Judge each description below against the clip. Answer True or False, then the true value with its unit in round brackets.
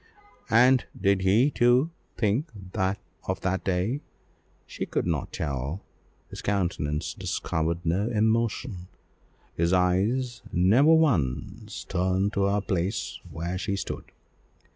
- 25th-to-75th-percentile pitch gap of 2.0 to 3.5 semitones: False (4.8 semitones)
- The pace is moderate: False (115 wpm)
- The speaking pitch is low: True (95 Hz)